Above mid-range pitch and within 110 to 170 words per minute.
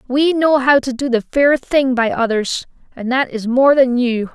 No: very high, 255 Hz; fast, 205 wpm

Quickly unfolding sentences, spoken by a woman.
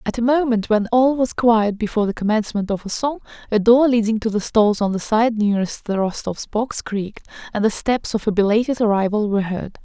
Yes: fast, 220 wpm; female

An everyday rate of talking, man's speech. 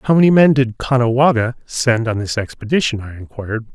Yes: average, 175 wpm; male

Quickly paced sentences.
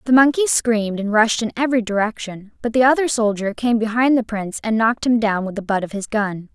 Yes: fast, 240 wpm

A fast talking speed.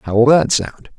Yes: fast, 245 wpm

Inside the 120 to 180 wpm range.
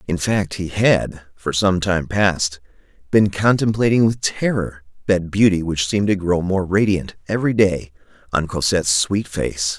Yes: average, 160 wpm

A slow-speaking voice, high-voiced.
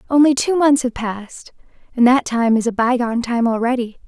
No: fast, 205 wpm; high, 245 Hz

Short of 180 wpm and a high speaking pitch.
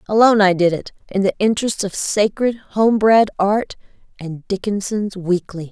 Yes: average, 160 wpm; high, 200 Hz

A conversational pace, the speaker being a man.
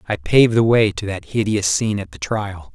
No: fast, 240 wpm; male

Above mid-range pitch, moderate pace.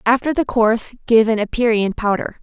Yes: high, 230 Hz; average, 175 wpm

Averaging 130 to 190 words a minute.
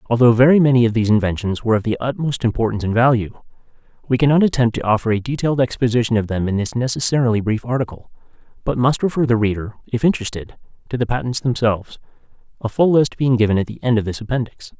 No: fast, 205 wpm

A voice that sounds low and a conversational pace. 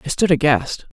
No: medium, 150 Hz; average, 190 wpm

